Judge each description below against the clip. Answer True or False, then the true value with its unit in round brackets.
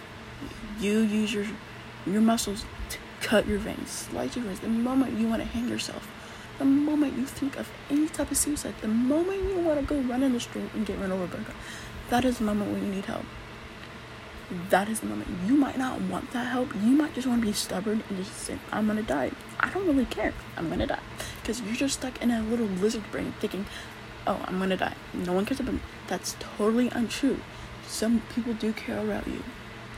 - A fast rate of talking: True (220 wpm)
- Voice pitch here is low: False (225 Hz)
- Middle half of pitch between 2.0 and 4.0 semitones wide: False (5.3 semitones)